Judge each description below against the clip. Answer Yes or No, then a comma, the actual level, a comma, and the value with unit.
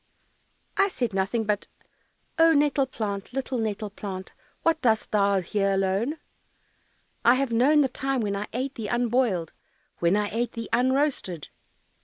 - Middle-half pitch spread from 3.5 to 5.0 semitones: Yes, average, 4.7 semitones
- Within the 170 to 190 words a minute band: No, average, 150 wpm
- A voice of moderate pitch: No, high, 230 Hz